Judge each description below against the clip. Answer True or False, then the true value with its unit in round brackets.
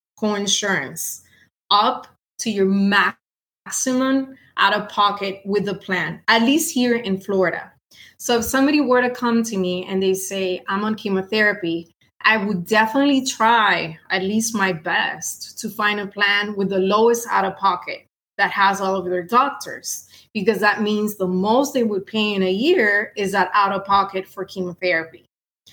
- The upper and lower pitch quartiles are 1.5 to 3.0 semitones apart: True (2.7 semitones)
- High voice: True (205 Hz)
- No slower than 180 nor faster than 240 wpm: False (170 wpm)